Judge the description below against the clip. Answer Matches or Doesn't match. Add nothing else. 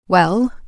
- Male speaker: Doesn't match